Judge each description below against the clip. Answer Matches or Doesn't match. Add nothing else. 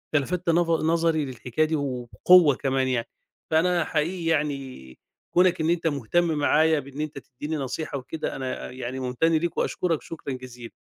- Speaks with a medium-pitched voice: Matches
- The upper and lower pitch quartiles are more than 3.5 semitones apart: Matches